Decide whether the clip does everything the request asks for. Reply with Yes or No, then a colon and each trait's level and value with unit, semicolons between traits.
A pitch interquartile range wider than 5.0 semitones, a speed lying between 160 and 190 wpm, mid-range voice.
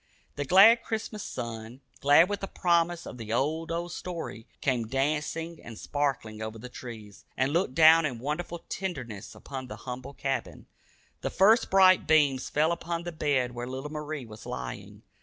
Yes: wide, 5.4 semitones; average, 170 wpm; medium, 145 Hz